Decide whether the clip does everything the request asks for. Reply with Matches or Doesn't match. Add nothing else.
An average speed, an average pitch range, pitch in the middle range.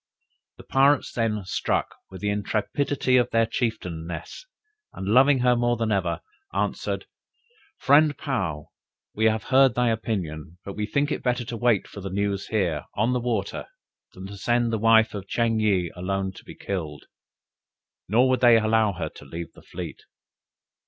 Doesn't match